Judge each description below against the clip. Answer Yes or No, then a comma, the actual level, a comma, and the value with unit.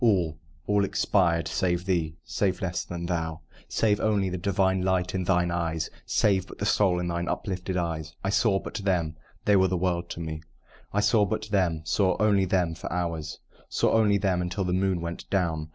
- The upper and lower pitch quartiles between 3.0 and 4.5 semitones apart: No, narrow, 2.4 semitones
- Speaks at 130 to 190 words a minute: No, average, 200 wpm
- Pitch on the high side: No, very low, 90 Hz